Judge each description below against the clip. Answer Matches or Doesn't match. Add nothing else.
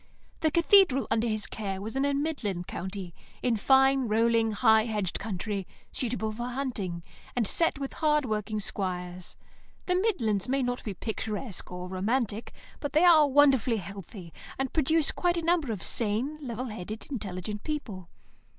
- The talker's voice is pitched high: Matches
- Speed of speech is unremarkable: Matches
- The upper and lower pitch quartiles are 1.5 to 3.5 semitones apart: Doesn't match